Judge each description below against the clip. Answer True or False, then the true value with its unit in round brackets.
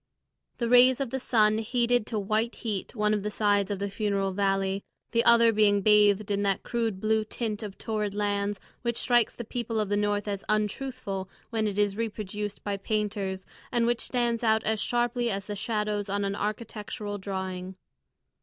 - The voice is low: False (210 Hz)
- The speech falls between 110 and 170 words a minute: False (185 wpm)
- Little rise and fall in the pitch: True (2.3 semitones)